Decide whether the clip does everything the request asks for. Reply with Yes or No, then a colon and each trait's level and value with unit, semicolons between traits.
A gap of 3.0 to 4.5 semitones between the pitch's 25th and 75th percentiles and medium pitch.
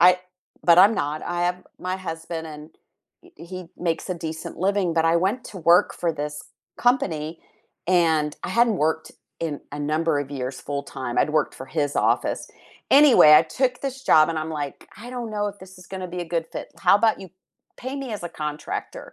Yes: average, 3.8 semitones; medium, 170 Hz